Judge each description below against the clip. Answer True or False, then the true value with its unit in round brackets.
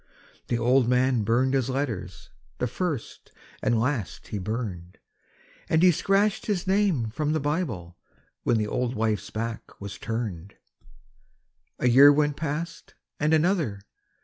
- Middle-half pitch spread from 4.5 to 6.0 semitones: True (5.6 semitones)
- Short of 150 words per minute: True (140 wpm)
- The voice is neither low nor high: False (125 Hz)